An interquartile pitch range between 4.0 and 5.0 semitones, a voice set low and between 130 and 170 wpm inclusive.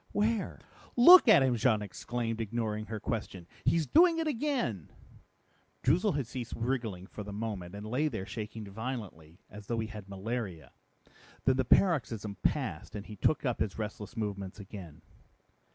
Yes: average, 4.4 semitones; low, 110 Hz; average, 160 wpm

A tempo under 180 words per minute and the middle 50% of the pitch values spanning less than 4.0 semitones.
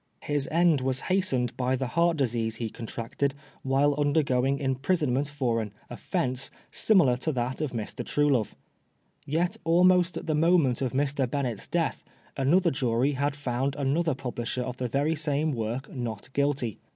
Yes: average, 165 wpm; average, 3.1 semitones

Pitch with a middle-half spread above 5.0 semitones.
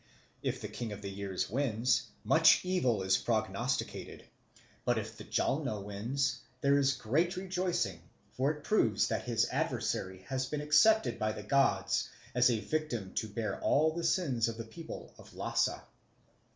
Yes: wide, 5.6 semitones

